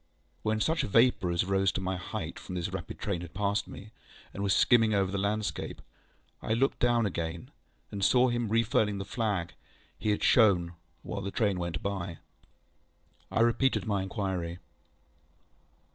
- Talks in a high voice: No, low, 100 Hz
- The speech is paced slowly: No, average, 165 wpm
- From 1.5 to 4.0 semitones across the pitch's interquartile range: Yes, average, 3.1 semitones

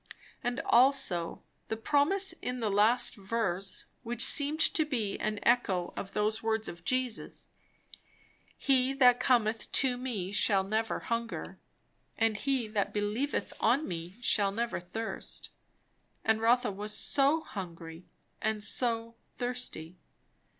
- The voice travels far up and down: No, average, 3.6 semitones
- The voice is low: No, high, 225 Hz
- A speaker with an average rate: No, slow, 130 wpm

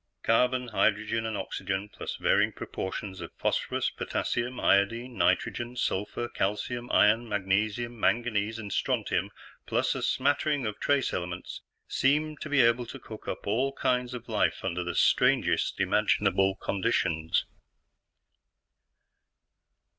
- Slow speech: Yes, slow, 125 wpm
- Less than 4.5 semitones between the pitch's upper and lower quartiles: Yes, average, 3.7 semitones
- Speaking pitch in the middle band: No, low, 110 Hz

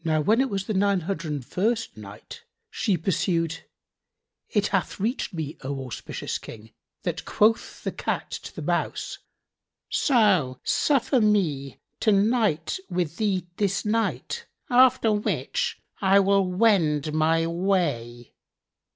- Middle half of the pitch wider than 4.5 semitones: Yes, average, 5.3 semitones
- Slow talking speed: Yes, slow, 130 wpm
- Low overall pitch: No, high, 190 Hz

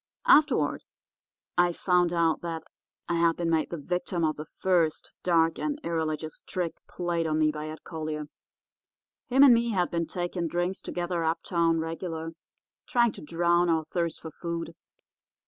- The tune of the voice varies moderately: No, narrow, 1.6 semitones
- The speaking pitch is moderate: Yes, medium, 170 Hz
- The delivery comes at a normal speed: Yes, average, 160 wpm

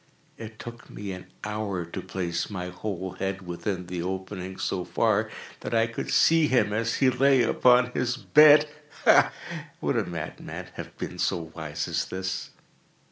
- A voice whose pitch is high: No, low, 100 Hz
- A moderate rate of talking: Yes, average, 160 wpm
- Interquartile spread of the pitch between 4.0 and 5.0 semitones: Yes, average, 4.7 semitones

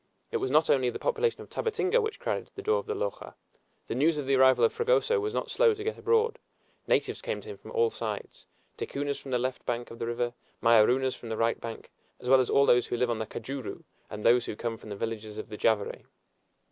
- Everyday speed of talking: No, fast, 245 wpm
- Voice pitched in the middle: No, low, 130 Hz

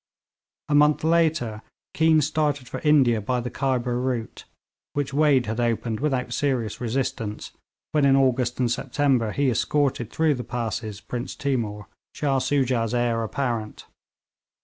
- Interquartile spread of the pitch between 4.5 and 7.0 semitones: No, average, 3.4 semitones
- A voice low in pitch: Yes, low, 125 Hz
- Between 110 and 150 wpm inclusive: Yes, average, 140 wpm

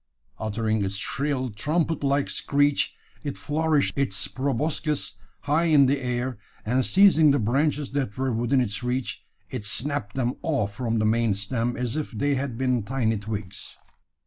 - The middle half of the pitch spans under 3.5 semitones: No, average, 4.2 semitones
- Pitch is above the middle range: No, low, 130 Hz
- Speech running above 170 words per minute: No, average, 160 wpm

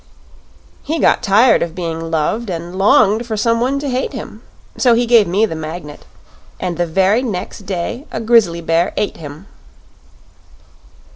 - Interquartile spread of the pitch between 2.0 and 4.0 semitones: No, wide, 5.4 semitones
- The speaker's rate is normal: Yes, average, 160 wpm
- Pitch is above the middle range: Yes, high, 195 Hz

